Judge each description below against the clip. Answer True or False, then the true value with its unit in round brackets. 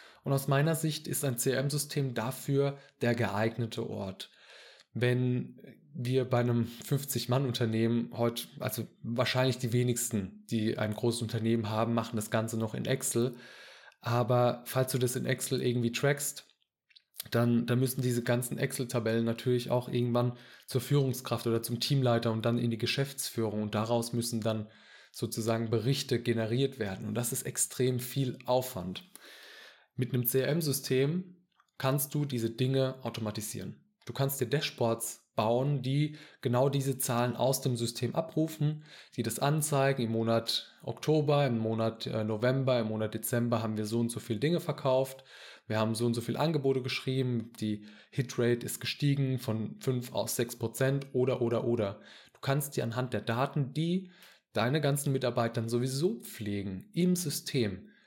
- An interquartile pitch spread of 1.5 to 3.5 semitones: True (2.8 semitones)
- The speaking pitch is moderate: False (125 Hz)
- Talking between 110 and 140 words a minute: False (155 wpm)